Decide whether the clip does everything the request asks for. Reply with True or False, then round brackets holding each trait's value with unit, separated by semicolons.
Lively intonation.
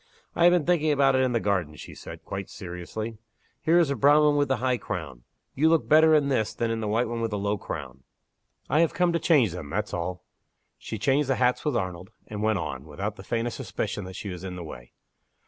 True (7.4 semitones)